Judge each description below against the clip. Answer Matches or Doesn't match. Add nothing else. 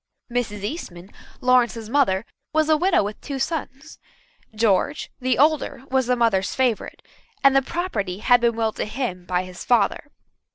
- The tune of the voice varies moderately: Matches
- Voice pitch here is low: Doesn't match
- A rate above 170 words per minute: Doesn't match